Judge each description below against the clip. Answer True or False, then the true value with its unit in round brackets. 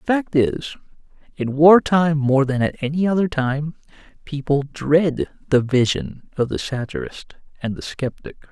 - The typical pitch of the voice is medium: True (145 Hz)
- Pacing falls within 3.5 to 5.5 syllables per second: True (4.4 syllables/s)